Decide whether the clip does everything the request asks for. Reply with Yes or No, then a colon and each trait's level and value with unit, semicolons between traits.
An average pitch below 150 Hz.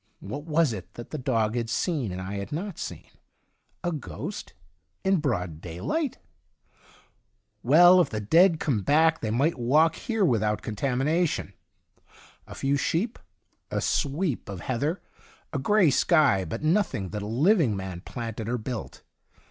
Yes: low, 135 Hz